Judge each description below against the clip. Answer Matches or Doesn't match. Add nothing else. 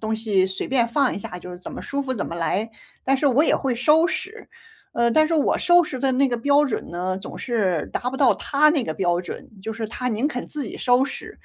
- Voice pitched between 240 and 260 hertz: Matches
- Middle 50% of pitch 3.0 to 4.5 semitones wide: Doesn't match